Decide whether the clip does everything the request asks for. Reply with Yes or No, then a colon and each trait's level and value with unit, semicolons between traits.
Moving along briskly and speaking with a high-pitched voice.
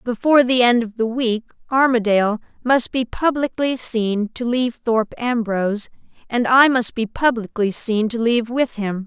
No: average, 165 wpm; high, 235 Hz